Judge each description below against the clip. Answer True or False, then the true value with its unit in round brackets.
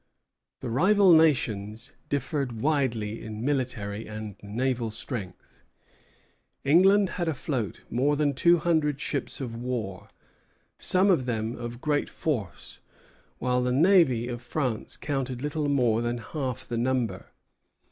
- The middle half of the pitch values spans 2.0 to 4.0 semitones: False (4.4 semitones)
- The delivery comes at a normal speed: False (125 wpm)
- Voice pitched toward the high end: False (125 Hz)